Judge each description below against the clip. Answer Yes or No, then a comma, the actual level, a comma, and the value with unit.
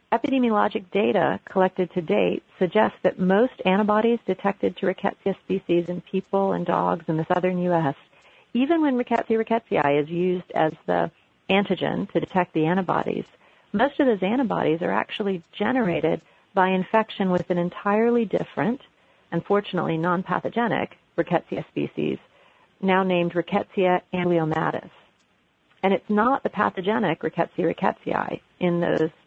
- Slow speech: Yes, slow, 130 wpm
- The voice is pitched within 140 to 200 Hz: Yes, medium, 185 Hz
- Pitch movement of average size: Yes, average, 3.6 semitones